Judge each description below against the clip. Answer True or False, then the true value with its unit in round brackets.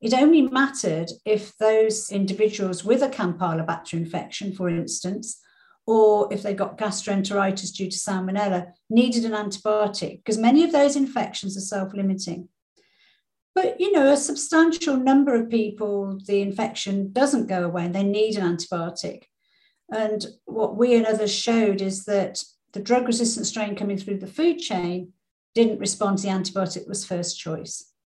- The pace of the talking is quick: False (155 wpm)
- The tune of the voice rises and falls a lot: False (3.5 semitones)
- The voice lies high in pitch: True (205 Hz)